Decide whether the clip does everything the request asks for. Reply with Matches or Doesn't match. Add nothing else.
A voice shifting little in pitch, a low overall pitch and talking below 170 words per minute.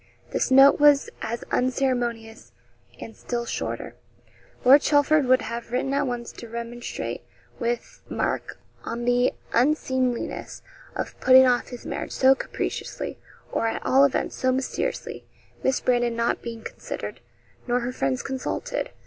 Doesn't match